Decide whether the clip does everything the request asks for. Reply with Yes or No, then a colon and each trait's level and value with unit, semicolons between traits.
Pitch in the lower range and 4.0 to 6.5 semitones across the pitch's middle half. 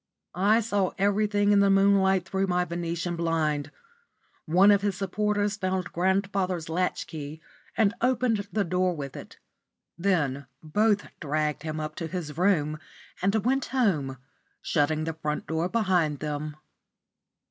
No: medium, 180 Hz; average, 4.4 semitones